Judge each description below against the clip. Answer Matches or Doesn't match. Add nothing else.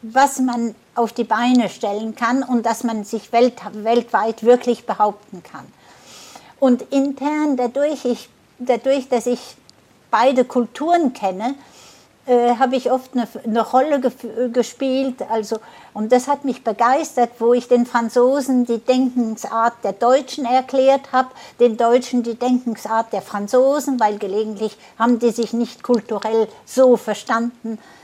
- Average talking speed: Matches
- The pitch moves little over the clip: Matches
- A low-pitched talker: Doesn't match